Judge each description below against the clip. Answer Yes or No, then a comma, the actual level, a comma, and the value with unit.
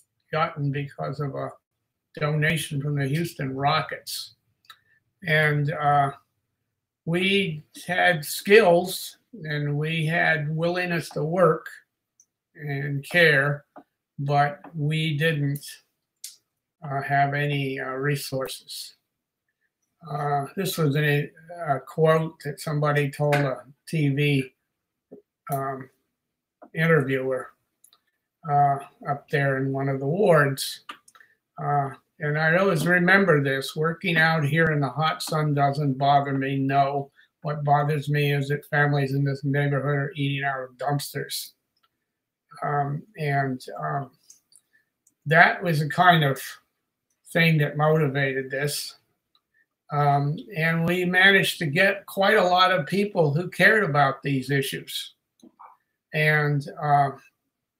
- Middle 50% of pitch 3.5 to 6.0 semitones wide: No, narrow, 2.6 semitones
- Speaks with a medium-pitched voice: Yes, medium, 145 Hz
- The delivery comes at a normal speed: No, slow, 115 wpm